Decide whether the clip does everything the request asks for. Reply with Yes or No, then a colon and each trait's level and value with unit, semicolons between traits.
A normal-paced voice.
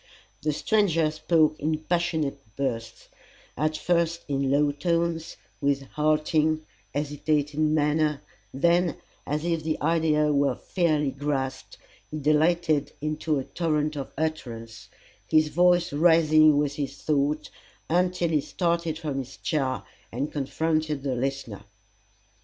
No: slow, 125 wpm